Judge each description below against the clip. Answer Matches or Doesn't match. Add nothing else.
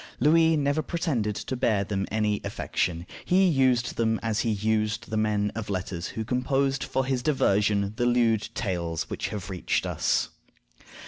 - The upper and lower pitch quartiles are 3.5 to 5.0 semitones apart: Matches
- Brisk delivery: Doesn't match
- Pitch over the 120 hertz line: Doesn't match